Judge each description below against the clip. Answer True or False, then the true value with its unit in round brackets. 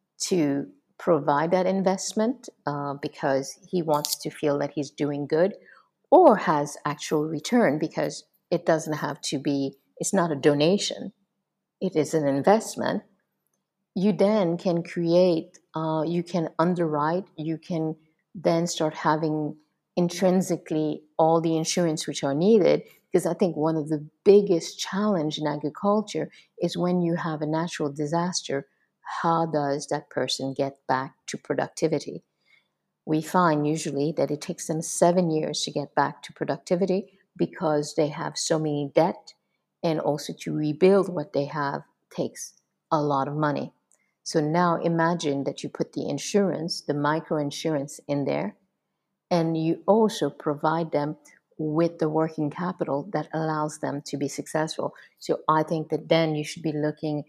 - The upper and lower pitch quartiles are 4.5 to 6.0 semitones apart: False (2.9 semitones)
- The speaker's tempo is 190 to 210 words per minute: False (155 wpm)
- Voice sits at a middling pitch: True (160 Hz)